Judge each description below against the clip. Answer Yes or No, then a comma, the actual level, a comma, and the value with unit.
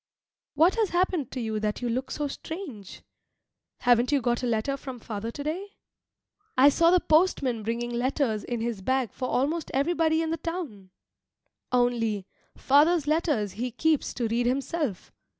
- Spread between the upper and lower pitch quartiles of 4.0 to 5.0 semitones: No, wide, 5.4 semitones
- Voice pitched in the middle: No, very high, 260 Hz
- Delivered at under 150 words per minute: No, average, 165 wpm